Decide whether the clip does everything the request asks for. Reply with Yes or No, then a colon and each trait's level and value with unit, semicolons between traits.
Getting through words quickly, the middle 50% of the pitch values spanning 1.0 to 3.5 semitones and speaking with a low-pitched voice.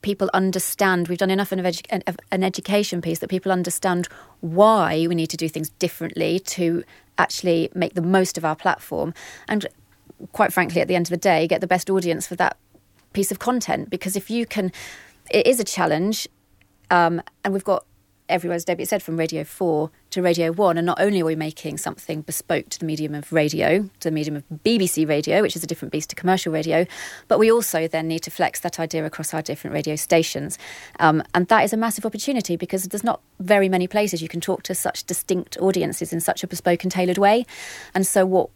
No: fast, 215 wpm; average, 2.8 semitones; medium, 180 Hz